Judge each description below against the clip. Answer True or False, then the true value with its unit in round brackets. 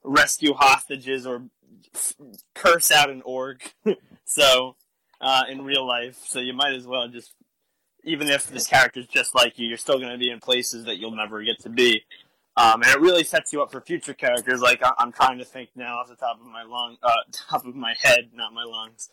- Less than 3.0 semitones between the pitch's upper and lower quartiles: True (2.6 semitones)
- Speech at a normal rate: False (220 wpm)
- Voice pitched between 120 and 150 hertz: True (125 Hz)